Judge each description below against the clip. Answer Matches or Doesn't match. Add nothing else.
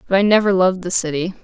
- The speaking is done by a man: Doesn't match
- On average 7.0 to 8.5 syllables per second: Matches